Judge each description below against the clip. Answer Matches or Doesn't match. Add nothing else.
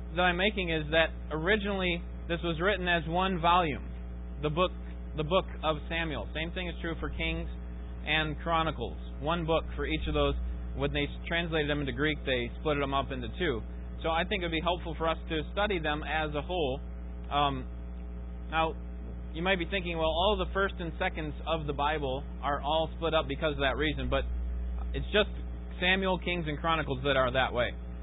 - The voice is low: Doesn't match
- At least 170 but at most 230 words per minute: Matches